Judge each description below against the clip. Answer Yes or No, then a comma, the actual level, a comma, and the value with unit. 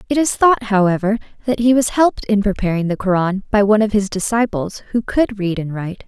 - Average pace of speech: No, fast, 215 wpm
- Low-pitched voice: No, high, 210 Hz